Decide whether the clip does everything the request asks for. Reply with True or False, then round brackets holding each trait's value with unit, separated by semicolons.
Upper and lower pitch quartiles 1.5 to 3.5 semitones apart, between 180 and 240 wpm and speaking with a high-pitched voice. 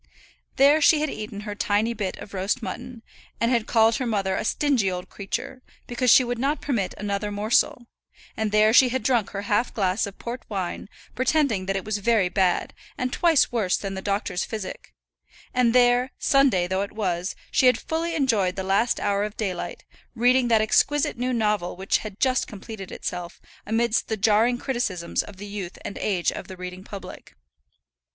False (4.0 semitones; 190 wpm; 215 Hz)